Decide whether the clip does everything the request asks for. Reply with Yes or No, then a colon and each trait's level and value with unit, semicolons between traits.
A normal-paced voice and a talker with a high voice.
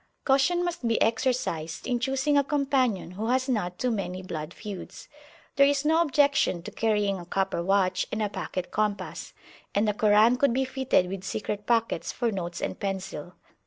Yes: average, 180 wpm; high, 215 Hz